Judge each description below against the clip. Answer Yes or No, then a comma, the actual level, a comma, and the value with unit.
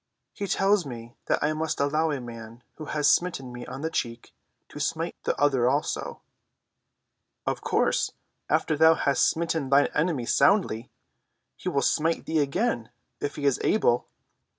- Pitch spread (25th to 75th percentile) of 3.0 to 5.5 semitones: Yes, average, 4.5 semitones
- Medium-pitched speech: Yes, medium, 145 Hz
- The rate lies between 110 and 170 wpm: Yes, average, 160 wpm